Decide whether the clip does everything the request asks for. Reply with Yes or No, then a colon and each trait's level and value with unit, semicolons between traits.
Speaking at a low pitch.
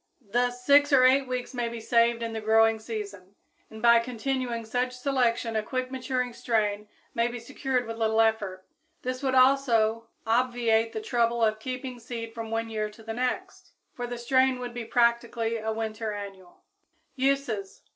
No: high, 235 Hz